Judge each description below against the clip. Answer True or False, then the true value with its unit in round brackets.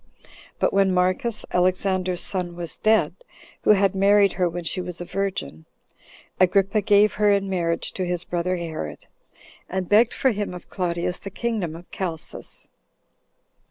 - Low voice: False (185 Hz)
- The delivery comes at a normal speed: True (155 wpm)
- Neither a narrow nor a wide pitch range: False (2.1 semitones)